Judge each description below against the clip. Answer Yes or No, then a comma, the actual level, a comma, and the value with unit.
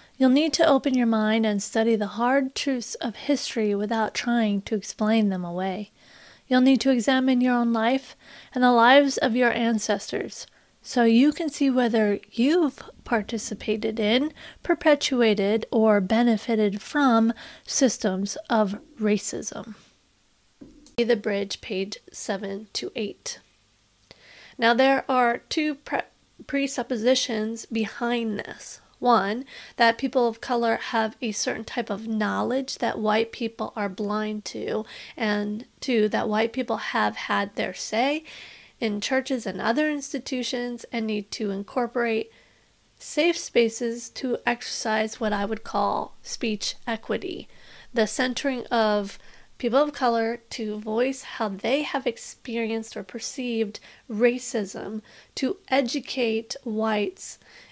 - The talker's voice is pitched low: No, high, 230 Hz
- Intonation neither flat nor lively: Yes, average, 3.1 semitones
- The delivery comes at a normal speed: No, slow, 130 wpm